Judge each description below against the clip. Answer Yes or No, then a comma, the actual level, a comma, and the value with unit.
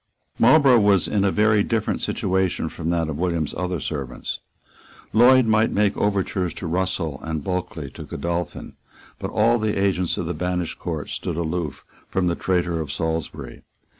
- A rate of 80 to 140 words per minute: No, average, 165 wpm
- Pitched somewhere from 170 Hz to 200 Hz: No, very low, 90 Hz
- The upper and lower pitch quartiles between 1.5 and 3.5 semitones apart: No, average, 3.9 semitones